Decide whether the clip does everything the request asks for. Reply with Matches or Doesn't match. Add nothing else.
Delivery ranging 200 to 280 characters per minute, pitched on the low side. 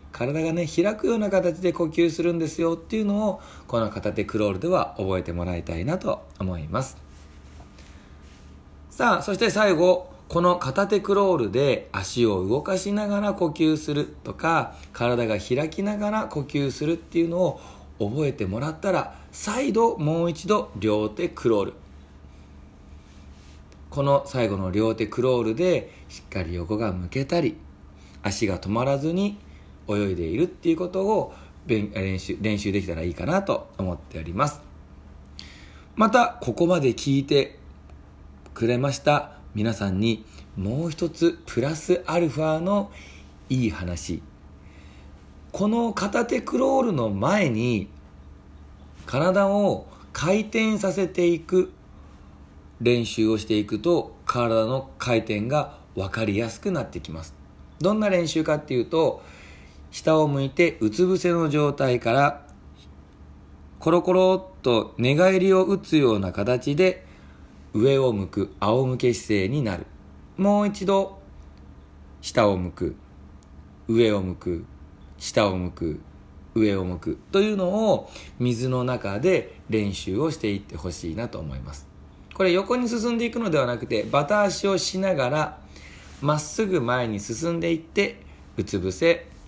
Matches